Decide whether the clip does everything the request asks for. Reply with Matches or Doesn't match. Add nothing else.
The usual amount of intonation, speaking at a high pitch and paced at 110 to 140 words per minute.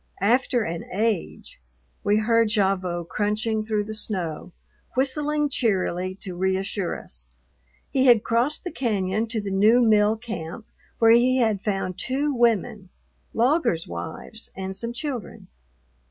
Matches